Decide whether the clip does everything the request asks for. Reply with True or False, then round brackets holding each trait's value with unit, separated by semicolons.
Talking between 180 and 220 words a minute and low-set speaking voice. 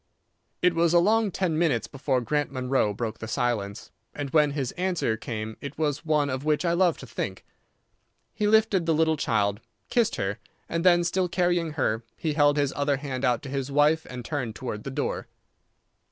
False (195 wpm; 145 Hz)